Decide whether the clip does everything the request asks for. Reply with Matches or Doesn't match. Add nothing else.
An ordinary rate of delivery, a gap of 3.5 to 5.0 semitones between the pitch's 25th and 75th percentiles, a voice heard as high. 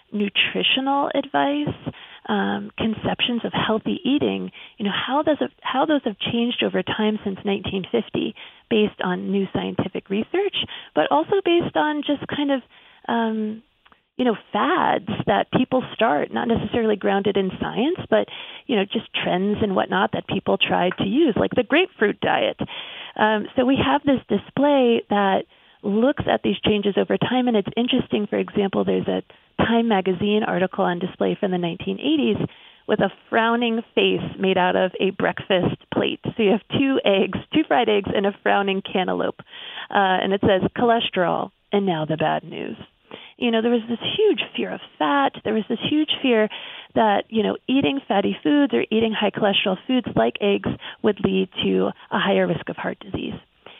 Matches